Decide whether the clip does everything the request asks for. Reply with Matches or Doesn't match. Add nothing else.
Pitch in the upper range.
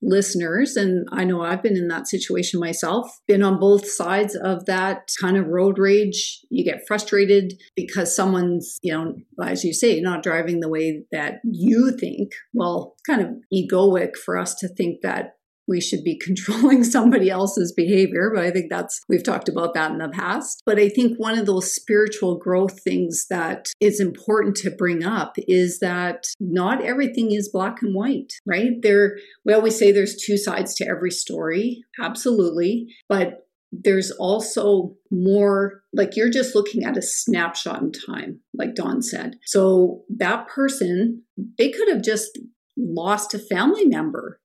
Matches